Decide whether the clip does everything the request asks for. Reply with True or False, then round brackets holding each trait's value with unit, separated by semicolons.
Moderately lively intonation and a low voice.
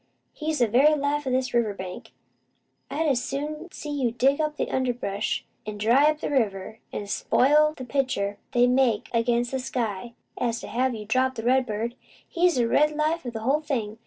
False (4.4 semitones; 255 Hz)